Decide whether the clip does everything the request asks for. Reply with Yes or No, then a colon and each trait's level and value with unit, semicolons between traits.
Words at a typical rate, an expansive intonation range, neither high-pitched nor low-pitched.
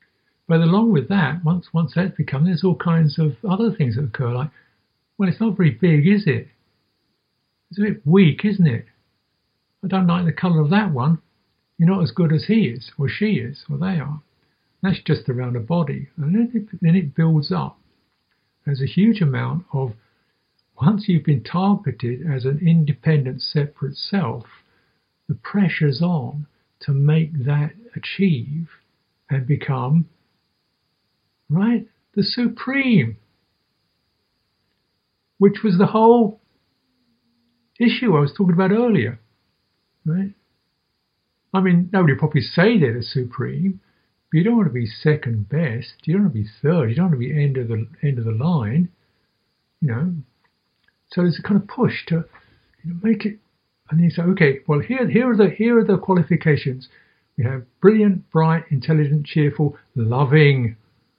Yes: average, 165 wpm; wide, 5.8 semitones; medium, 160 Hz